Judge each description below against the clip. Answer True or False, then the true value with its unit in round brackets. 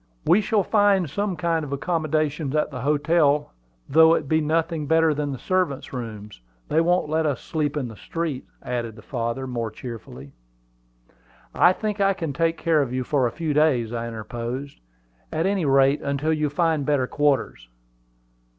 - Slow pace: False (175 wpm)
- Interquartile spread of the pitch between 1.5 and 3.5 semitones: False (4.2 semitones)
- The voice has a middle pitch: True (150 Hz)